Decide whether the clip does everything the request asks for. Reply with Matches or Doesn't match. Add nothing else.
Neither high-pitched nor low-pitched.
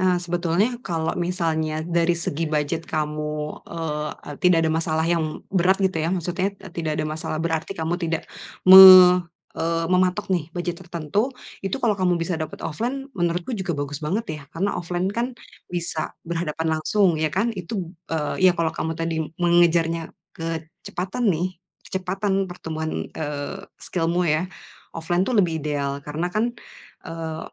Matches